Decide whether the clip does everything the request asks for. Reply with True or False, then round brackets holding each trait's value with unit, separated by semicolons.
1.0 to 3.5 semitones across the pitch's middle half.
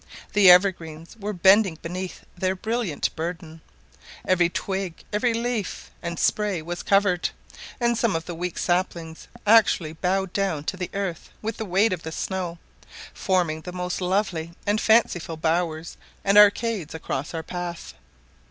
True (3.2 semitones)